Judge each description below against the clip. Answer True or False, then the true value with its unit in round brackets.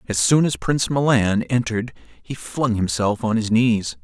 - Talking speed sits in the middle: True (180 wpm)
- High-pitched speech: False (115 Hz)